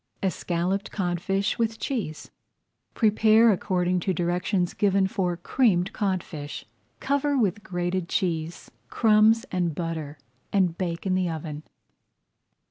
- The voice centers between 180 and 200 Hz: Yes, medium, 185 Hz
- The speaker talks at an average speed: No, slow, 115 wpm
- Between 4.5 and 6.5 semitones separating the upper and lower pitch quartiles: No, average, 3.2 semitones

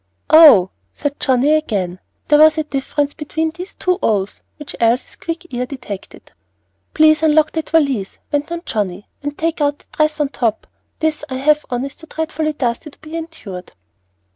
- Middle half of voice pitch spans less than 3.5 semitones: No, average, 4.2 semitones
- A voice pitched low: No, very high, 295 Hz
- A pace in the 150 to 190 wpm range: Yes, average, 175 wpm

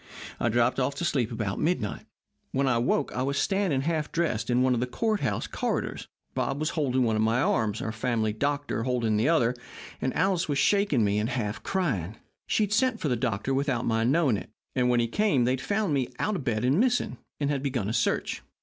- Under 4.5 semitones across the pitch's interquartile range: No, average, 5.0 semitones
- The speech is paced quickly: Yes, fast, 225 wpm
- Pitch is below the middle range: Yes, low, 130 Hz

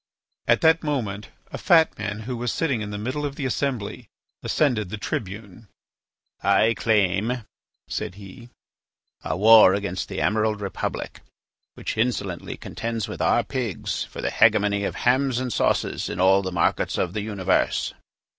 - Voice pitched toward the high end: No, low, 110 Hz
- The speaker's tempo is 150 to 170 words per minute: Yes, average, 155 wpm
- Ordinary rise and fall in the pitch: Yes, average, 3.7 semitones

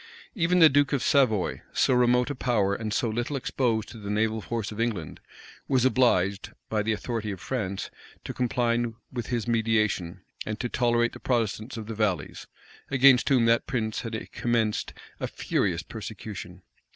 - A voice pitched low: Yes, low, 115 Hz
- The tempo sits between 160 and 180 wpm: Yes, average, 170 wpm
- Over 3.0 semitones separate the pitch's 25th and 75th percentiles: No, average, 2.7 semitones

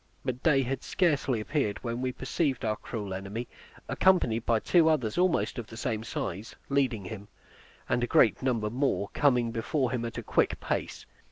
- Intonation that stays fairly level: No, average, 3.7 semitones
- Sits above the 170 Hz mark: No, low, 120 Hz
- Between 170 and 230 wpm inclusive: Yes, average, 180 wpm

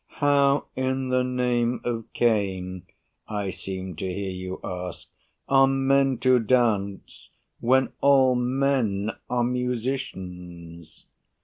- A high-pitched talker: No, low, 120 Hz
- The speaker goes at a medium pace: No, slow, 110 wpm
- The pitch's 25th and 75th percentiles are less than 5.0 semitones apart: No, wide, 5.6 semitones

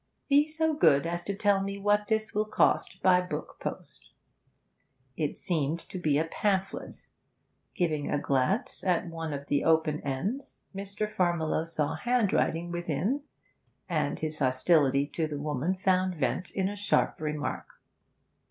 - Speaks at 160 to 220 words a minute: No, average, 150 wpm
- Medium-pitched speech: Yes, medium, 175 Hz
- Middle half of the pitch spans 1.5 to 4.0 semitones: No, average, 4.7 semitones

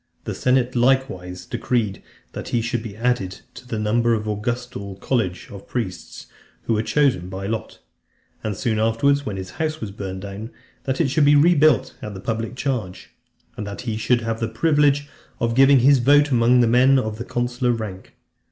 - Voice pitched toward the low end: Yes, low, 115 Hz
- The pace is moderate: Yes, average, 190 wpm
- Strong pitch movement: No, average, 3.8 semitones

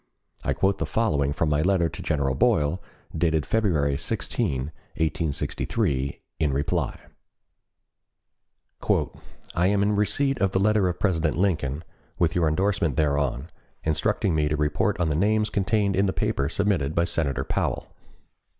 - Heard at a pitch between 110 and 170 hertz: No, very low, 80 Hz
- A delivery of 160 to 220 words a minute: No, average, 145 wpm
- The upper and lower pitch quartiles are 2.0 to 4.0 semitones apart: No, average, 5.0 semitones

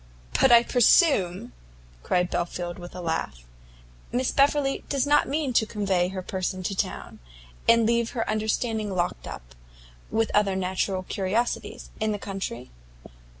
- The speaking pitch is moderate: No, high, 200 Hz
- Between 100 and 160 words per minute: Yes, average, 145 wpm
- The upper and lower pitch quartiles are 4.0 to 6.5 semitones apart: Yes, average, 4.6 semitones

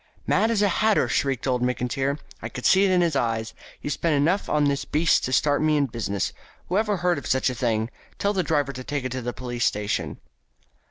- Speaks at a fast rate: Yes, fast, 230 wpm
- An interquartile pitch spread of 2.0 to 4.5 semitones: No, wide, 5.4 semitones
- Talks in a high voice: No, medium, 140 Hz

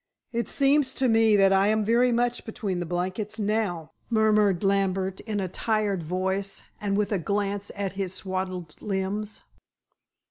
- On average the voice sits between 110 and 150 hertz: No, high, 200 Hz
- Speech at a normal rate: Yes, average, 155 wpm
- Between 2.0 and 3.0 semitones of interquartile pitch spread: Yes, narrow, 2.4 semitones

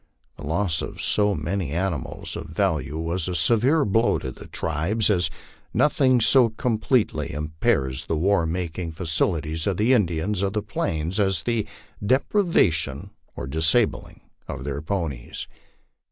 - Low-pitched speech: Yes, very low, 90 Hz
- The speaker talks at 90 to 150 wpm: Yes, average, 140 wpm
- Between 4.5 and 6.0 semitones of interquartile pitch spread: Yes, average, 5.2 semitones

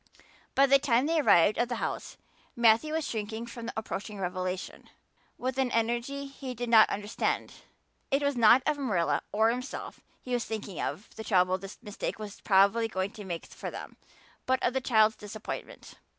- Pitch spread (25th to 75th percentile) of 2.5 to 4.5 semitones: Yes, average, 3.8 semitones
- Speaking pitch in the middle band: No, high, 225 Hz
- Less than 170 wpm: No, average, 185 wpm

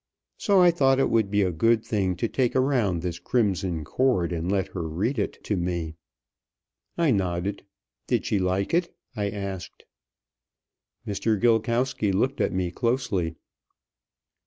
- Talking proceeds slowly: No, average, 150 wpm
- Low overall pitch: Yes, low, 100 Hz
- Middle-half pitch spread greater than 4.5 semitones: Yes, average, 5.1 semitones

